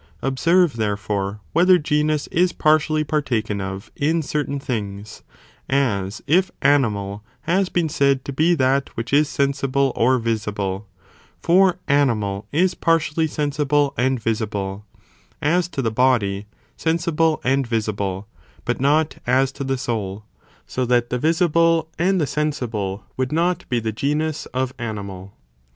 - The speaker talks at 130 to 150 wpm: Yes, average, 140 wpm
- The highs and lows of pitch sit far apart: Yes, wide, 6.1 semitones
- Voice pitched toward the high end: No, low, 135 Hz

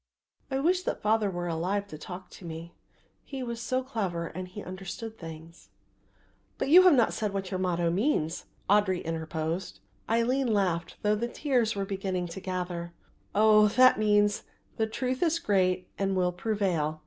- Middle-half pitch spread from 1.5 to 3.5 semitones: No, average, 4.3 semitones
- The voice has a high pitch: Yes, high, 195 Hz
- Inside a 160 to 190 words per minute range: Yes, average, 170 wpm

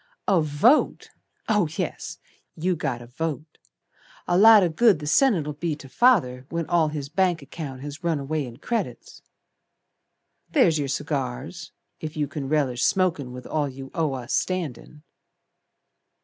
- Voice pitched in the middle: Yes, medium, 155 Hz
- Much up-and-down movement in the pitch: No, average, 4.2 semitones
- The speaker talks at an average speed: Yes, average, 150 wpm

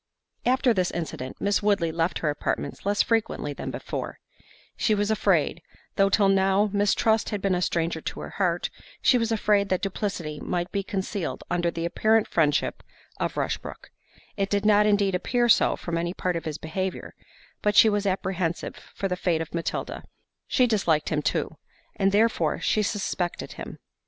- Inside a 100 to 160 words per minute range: No, average, 170 wpm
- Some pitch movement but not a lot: Yes, average, 3.5 semitones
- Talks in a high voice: Yes, high, 195 Hz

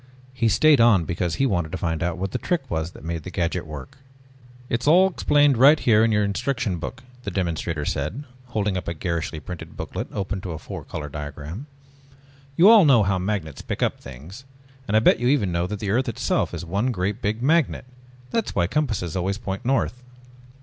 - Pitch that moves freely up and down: Yes, wide, 6.5 semitones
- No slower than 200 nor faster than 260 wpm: Yes, fast, 205 wpm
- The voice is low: Yes, low, 100 Hz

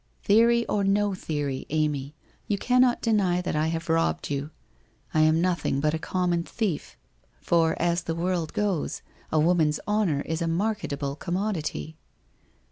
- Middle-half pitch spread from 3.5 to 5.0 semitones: Yes, average, 4.4 semitones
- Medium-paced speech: Yes, average, 155 wpm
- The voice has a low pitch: No, medium, 170 Hz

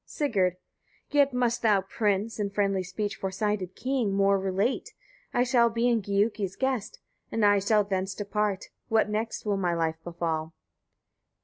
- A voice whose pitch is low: No, high, 205 Hz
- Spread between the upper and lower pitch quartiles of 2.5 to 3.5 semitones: Yes, average, 3.0 semitones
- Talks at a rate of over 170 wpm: No, average, 150 wpm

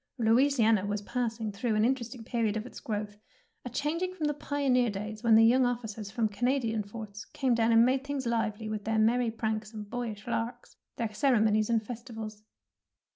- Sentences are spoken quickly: No, average, 180 wpm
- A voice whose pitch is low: No, high, 225 Hz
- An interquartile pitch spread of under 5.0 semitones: Yes, narrow, 2.4 semitones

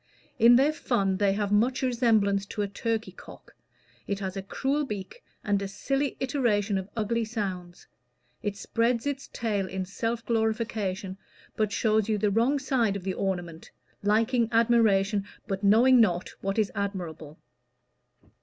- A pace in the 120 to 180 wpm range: Yes, average, 155 wpm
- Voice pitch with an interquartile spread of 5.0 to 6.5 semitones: No, average, 3.0 semitones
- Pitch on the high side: Yes, high, 210 Hz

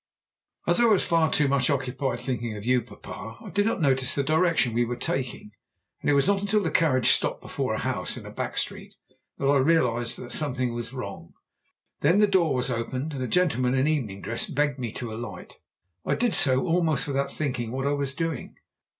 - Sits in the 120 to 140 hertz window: Yes, low, 135 Hz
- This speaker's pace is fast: Yes, fast, 210 wpm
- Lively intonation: No, average, 4.3 semitones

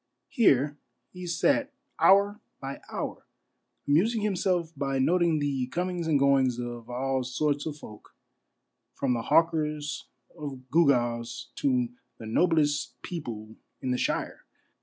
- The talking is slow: Yes, slow, 125 wpm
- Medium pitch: Yes, medium, 145 Hz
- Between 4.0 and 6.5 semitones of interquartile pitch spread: Yes, average, 5.2 semitones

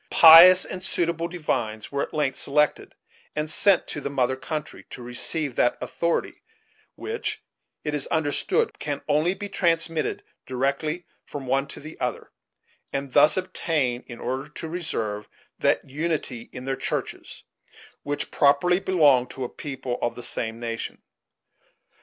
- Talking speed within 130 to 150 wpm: Yes, average, 145 wpm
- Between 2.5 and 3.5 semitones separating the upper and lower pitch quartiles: No, average, 4.3 semitones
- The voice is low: No, medium, 145 Hz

